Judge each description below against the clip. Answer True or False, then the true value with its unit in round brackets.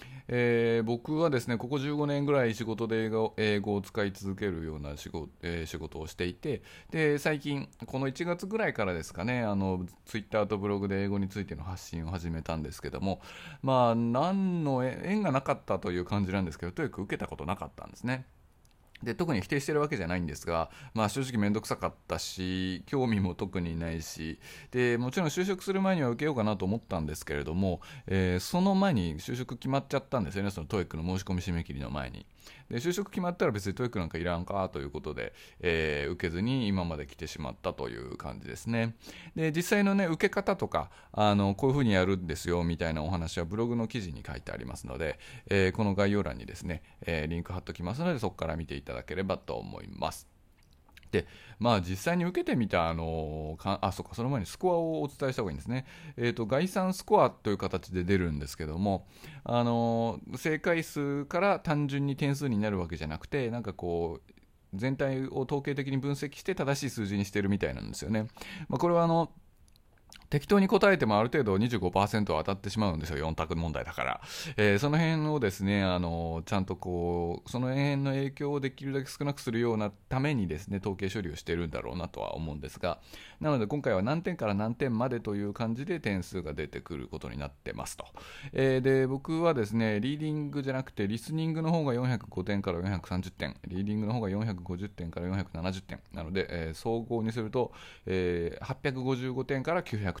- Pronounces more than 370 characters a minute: True (410 characters per minute)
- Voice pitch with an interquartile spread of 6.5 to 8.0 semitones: True (7.3 semitones)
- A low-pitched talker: True (105 Hz)